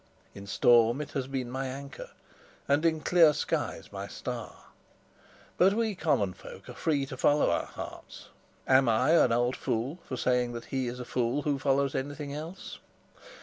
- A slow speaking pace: No, average, 175 wpm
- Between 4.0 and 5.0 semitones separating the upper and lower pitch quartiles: No, average, 3.3 semitones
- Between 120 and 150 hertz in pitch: Yes, low, 135 Hz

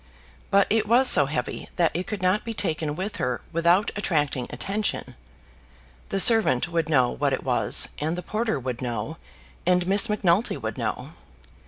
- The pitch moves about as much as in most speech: No, wide, 5.9 semitones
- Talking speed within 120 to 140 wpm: No, average, 170 wpm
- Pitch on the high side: No, medium, 175 Hz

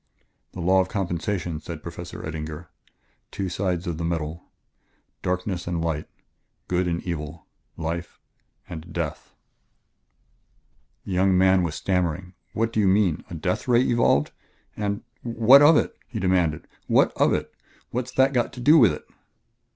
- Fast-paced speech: No, average, 150 wpm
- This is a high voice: No, very low, 90 Hz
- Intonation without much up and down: No, average, 3.5 semitones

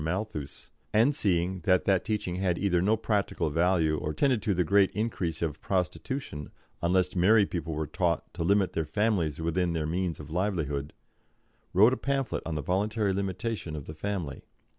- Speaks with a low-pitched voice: Yes, very low, 90 Hz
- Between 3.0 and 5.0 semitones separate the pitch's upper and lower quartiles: Yes, average, 4.1 semitones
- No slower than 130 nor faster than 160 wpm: No, average, 175 wpm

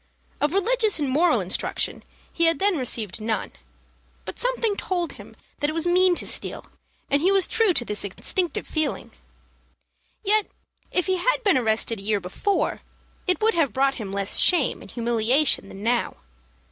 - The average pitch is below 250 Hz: No, very high, 315 Hz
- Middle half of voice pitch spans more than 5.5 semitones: Yes, wide, 8.5 semitones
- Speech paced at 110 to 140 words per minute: No, average, 170 wpm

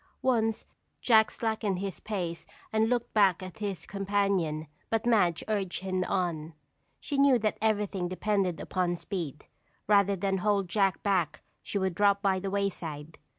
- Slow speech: No, average, 150 wpm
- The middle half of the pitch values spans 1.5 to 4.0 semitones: Yes, average, 2.9 semitones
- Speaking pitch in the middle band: No, high, 195 Hz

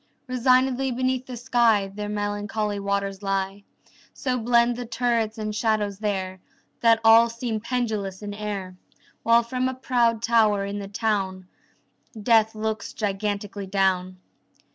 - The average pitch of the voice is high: Yes, high, 215 Hz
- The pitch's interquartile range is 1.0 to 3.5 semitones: Yes, average, 2.9 semitones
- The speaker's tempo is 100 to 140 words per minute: Yes, slow, 135 wpm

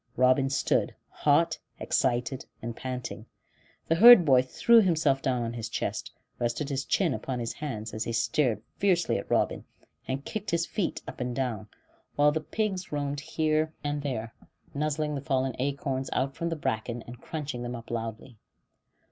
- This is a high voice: No, low, 135 Hz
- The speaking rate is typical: Yes, average, 170 wpm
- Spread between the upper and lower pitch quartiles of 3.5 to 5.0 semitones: Yes, average, 4.0 semitones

